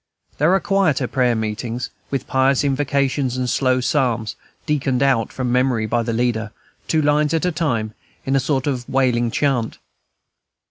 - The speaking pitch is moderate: No, low, 130 Hz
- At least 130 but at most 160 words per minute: No, average, 170 wpm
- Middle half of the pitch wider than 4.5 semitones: No, average, 2.8 semitones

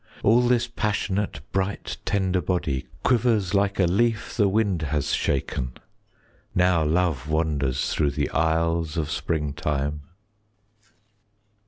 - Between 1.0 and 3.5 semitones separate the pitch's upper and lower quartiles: No, average, 5.0 semitones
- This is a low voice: Yes, very low, 85 Hz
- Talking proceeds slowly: Yes, slow, 115 wpm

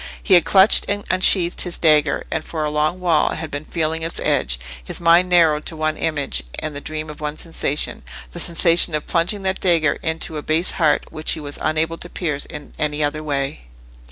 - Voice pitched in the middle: Yes, medium, 155 Hz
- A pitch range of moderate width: No, narrow, 2.2 semitones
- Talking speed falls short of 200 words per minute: No, fast, 205 wpm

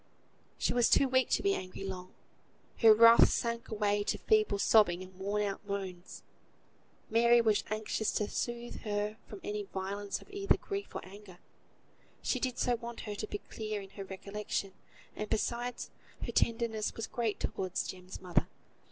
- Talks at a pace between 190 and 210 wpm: No, average, 170 wpm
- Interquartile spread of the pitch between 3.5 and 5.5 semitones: No, average, 3.1 semitones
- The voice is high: Yes, high, 210 Hz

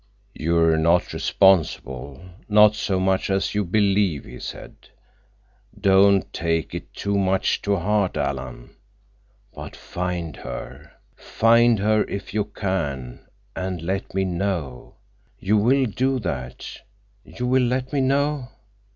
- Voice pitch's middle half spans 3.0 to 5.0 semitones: Yes, average, 4.1 semitones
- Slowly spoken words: Yes, slow, 120 wpm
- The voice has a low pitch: Yes, very low, 95 Hz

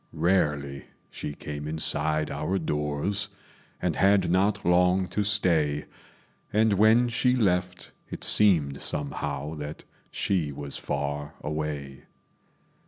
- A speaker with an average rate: No, slow, 110 wpm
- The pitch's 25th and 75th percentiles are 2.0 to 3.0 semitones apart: No, average, 4.9 semitones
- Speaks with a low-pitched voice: Yes, very low, 80 Hz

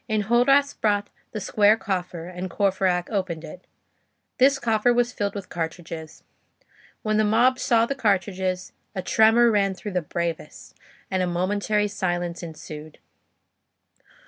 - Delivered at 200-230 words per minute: No, slow, 135 wpm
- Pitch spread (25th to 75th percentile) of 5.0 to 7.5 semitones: No, average, 3.6 semitones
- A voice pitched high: Yes, high, 195 Hz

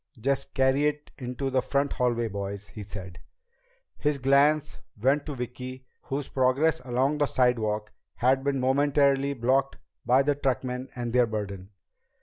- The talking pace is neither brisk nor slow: Yes, average, 145 wpm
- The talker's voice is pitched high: No, low, 130 Hz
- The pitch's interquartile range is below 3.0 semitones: Yes, narrow, 2.6 semitones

